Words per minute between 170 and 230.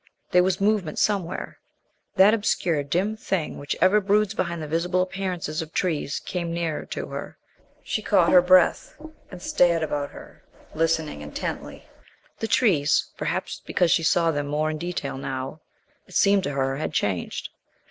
No: average, 160 wpm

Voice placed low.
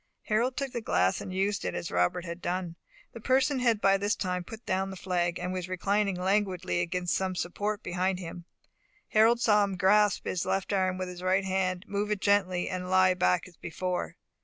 No: medium, 185 Hz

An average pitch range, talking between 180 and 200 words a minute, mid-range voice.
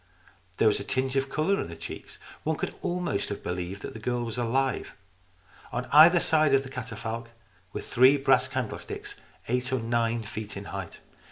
No: average, 3.5 semitones; average, 185 wpm; low, 120 Hz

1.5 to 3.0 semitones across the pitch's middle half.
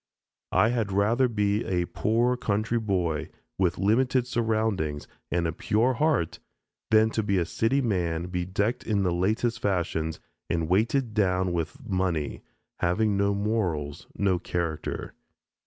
No: average, 4.2 semitones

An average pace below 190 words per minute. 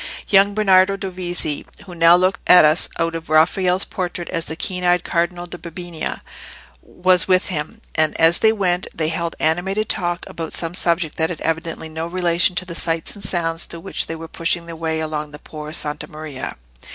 No: average, 195 wpm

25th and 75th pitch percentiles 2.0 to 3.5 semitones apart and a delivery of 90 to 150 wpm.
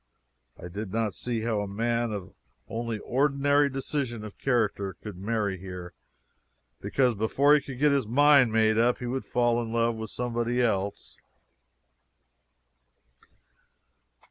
Yes: average, 3.1 semitones; average, 140 wpm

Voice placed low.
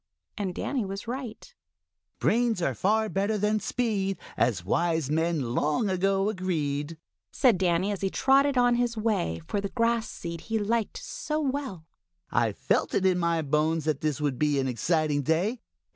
No: high, 190 Hz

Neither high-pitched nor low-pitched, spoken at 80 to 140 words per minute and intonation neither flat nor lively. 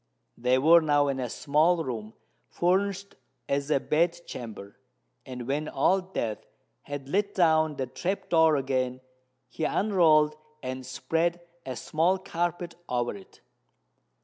Yes: medium, 150 Hz; slow, 135 wpm; average, 5.0 semitones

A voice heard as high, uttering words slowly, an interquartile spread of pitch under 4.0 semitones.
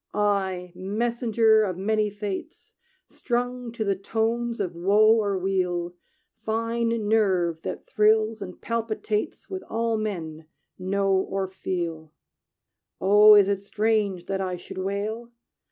Yes: high, 205 Hz; slow, 125 wpm; average, 2.8 semitones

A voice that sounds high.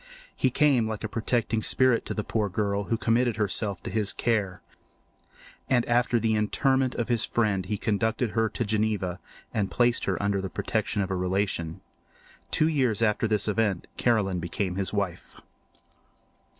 No: low, 110 Hz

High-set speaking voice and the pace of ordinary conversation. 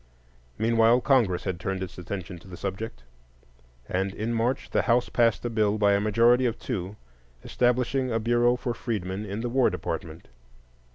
No: low, 110 Hz; average, 170 wpm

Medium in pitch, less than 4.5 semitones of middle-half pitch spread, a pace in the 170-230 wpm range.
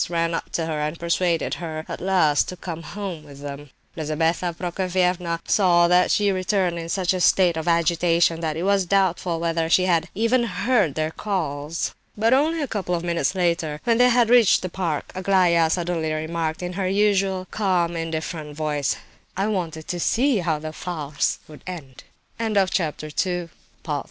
Yes: medium, 175 Hz; average, 2.8 semitones; average, 175 wpm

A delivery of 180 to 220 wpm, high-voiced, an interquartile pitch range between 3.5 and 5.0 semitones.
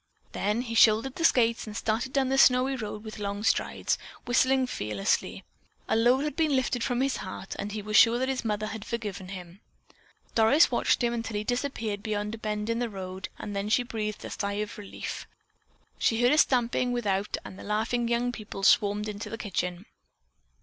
No: average, 200 wpm; high, 220 Hz; average, 2.9 semitones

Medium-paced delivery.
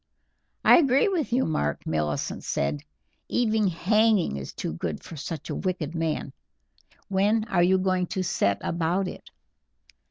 Yes: average, 150 wpm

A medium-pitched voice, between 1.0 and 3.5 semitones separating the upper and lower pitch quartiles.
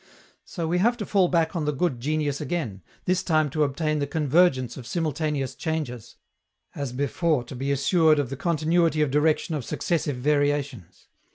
Yes: medium, 150 Hz; average, 3.1 semitones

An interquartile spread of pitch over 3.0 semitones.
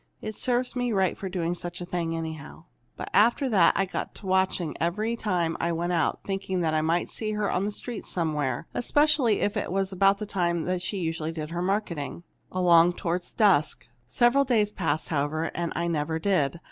Yes: average, 3.8 semitones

